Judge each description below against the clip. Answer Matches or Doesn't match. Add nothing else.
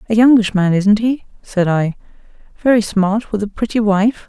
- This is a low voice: Doesn't match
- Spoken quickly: Doesn't match